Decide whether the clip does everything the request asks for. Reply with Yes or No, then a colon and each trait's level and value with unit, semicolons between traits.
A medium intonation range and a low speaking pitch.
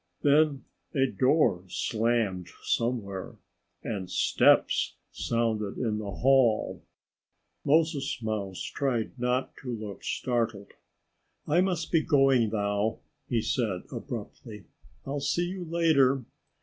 Yes: average, 4.7 semitones; low, 120 Hz